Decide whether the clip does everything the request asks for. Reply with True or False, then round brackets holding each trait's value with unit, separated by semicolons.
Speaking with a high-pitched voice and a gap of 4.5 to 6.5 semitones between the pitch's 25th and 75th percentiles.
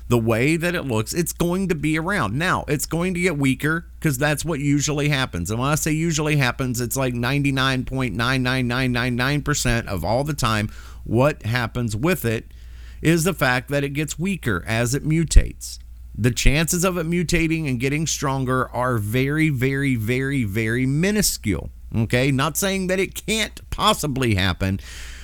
False (135 Hz; 4.8 semitones)